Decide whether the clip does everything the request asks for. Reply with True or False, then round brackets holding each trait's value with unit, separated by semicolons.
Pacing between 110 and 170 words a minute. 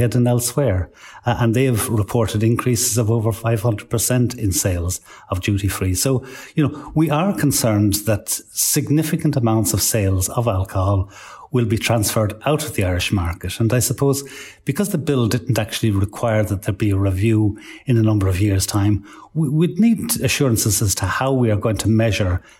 False (180 wpm)